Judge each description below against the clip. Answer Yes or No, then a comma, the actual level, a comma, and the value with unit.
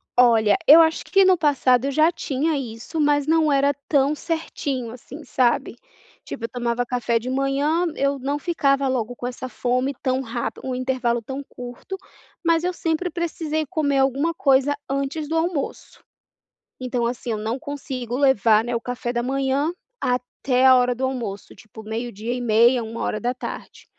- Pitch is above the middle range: Yes, very high, 265 Hz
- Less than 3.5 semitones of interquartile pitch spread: Yes, average, 3.1 semitones